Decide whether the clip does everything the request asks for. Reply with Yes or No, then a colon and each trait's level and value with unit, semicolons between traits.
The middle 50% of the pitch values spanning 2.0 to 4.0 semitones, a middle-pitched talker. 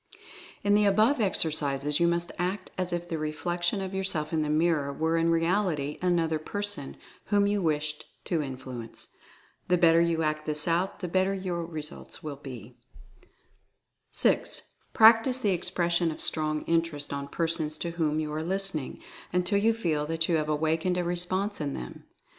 Yes: average, 3.3 semitones; medium, 165 Hz